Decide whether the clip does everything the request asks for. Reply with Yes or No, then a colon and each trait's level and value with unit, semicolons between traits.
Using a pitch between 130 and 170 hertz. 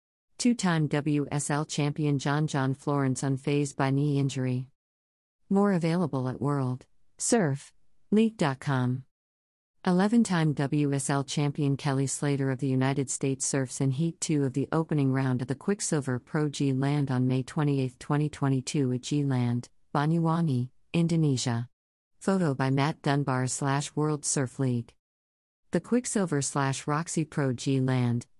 Yes: medium, 140 Hz